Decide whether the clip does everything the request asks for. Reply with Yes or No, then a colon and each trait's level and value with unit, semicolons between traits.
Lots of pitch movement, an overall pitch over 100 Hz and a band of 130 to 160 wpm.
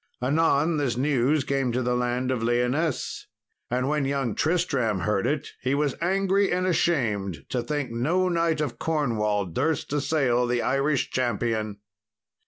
No: average, 4.2 semitones; low, 135 Hz; average, 150 wpm